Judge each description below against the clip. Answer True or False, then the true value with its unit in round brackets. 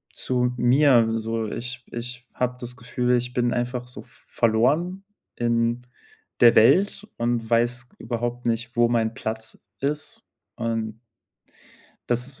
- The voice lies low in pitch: True (120 Hz)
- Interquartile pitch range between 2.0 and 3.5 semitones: False (1.2 semitones)